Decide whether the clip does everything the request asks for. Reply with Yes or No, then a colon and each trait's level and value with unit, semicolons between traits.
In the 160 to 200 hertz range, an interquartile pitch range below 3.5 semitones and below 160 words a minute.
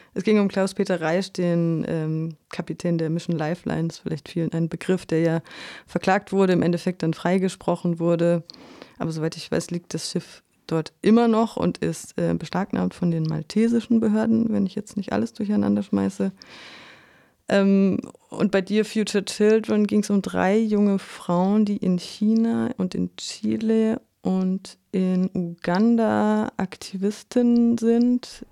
No: high, 190 Hz; average, 4.5 semitones; average, 150 wpm